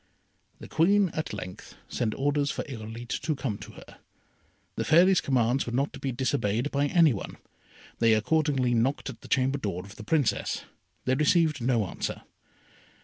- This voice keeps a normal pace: Yes, average, 170 wpm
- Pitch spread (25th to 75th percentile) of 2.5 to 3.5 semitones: No, average, 4.5 semitones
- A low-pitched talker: Yes, low, 130 Hz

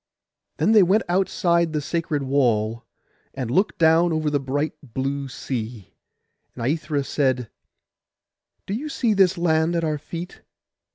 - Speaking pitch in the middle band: Yes, medium, 155 Hz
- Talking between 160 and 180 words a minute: No, average, 140 wpm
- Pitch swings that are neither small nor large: Yes, average, 4.3 semitones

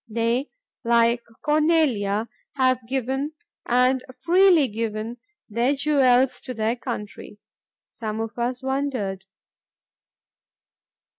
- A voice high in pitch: Yes, very high, 250 Hz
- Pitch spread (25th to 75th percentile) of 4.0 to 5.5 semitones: No, average, 3.1 semitones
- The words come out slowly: Yes, slow, 90 wpm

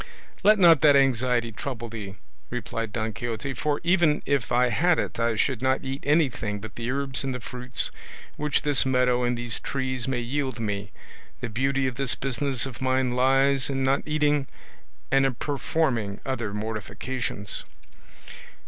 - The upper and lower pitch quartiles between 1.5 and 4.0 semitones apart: Yes, average, 2.8 semitones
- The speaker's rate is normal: Yes, average, 165 wpm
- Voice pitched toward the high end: No, low, 130 Hz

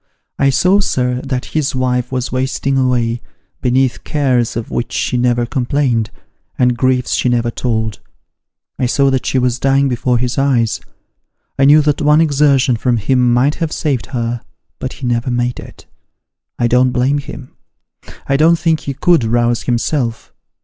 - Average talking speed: Yes, average, 165 wpm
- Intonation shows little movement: Yes, narrow, 2.3 semitones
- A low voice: Yes, low, 125 Hz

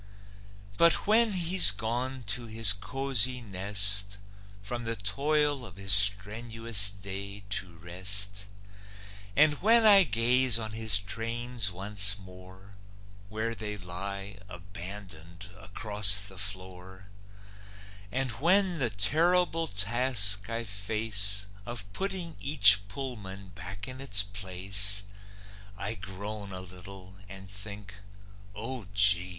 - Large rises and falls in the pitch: No, average, 3.4 semitones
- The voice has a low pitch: Yes, low, 105 Hz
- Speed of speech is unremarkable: No, slow, 115 wpm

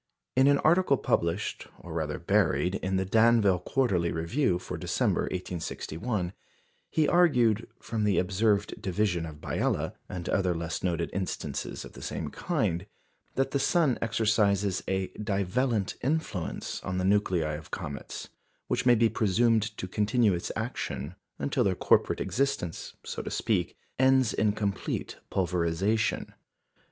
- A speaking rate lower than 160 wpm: Yes, average, 140 wpm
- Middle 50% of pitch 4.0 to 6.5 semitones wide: Yes, average, 4.8 semitones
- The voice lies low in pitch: Yes, low, 100 Hz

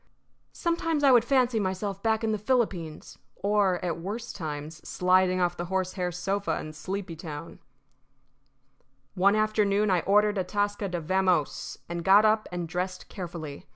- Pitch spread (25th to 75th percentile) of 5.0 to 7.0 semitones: No, average, 3.2 semitones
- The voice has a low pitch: No, high, 190 Hz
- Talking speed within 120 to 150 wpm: Yes, average, 145 wpm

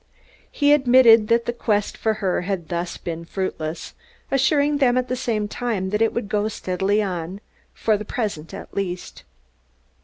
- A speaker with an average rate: Yes, average, 175 wpm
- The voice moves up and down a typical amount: Yes, average, 4.6 semitones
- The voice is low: No, high, 210 Hz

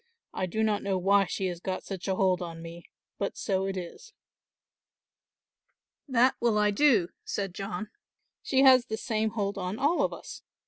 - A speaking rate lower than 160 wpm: No, average, 180 wpm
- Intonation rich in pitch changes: No, average, 2.9 semitones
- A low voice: No, high, 200 Hz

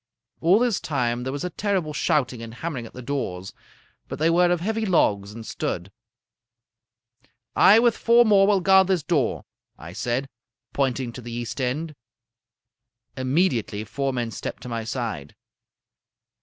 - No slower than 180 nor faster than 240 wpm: No, average, 155 wpm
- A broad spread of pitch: Yes, wide, 7.2 semitones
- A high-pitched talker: No, low, 135 Hz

